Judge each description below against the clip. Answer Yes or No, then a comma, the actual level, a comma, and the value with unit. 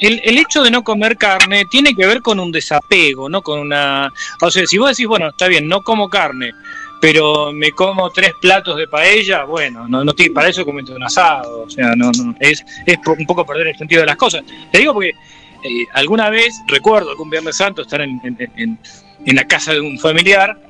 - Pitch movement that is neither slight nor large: No, wide, 6.1 semitones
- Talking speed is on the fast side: Yes, fast, 225 wpm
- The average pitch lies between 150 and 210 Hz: Yes, medium, 185 Hz